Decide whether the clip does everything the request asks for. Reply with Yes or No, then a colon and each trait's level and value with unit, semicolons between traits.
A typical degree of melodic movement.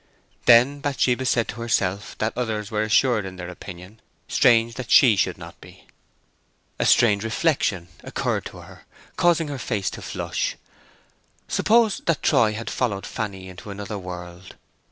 Yes: average, 4.3 semitones